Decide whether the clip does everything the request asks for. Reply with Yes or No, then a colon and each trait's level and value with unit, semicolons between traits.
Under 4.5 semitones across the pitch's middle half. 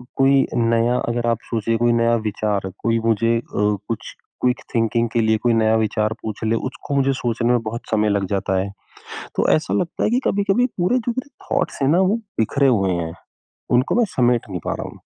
Yes: average, 3.4 semitones